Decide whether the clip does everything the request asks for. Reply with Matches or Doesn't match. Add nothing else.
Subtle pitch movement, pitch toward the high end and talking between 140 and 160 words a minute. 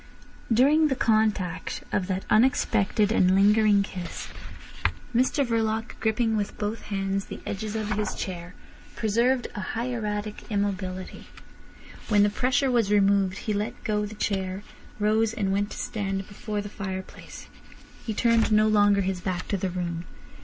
Matches